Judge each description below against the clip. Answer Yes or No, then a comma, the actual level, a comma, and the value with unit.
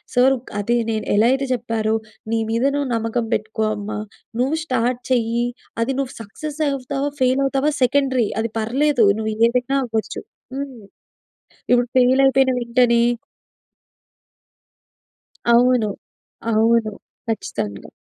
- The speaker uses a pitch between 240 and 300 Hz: Yes, high, 245 Hz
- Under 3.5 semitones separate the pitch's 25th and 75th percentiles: Yes, average, 2.9 semitones